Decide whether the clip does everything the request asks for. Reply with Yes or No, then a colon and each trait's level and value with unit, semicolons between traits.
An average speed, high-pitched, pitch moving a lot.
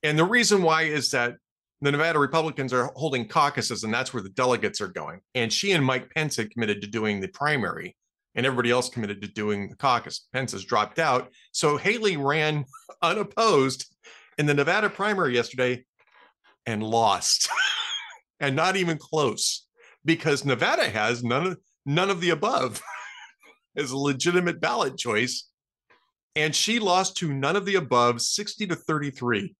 No: average, 165 wpm; medium, 140 Hz; wide, 5.7 semitones